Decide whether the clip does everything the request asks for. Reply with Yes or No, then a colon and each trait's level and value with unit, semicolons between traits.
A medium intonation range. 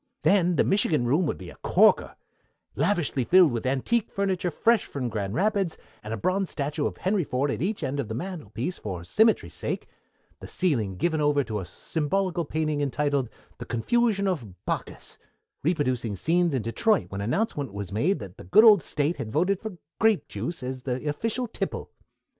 No: wide, 7.5 semitones